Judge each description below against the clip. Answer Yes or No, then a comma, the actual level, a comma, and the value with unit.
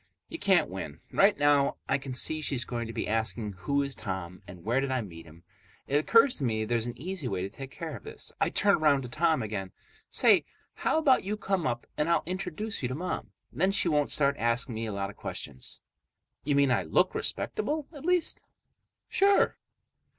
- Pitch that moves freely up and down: Yes, wide, 7.8 semitones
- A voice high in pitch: No, medium, 140 Hz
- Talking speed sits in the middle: No, fast, 210 wpm